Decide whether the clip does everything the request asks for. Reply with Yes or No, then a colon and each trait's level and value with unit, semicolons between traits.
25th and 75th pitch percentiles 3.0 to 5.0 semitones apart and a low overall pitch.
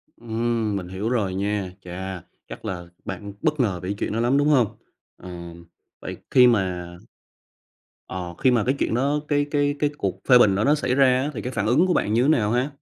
No: wide, 5.6 semitones; low, 115 Hz